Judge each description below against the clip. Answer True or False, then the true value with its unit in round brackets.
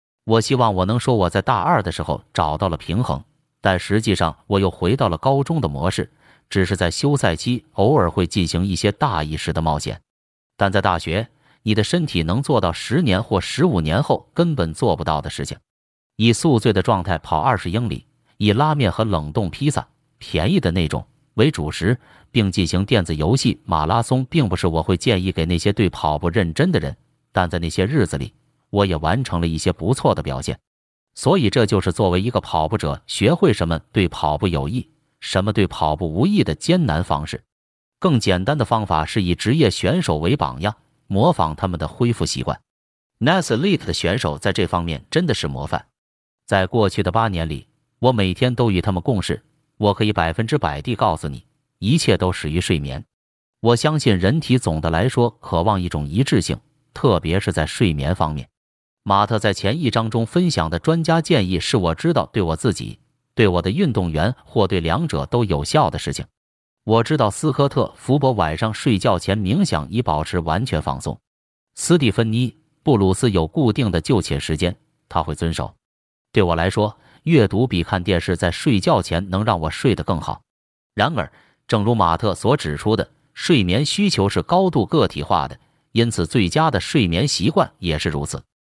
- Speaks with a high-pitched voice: False (100 Hz)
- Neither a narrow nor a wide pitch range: False (6.1 semitones)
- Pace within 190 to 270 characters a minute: False (285 characters per minute)